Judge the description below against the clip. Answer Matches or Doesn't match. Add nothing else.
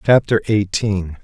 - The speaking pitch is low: Matches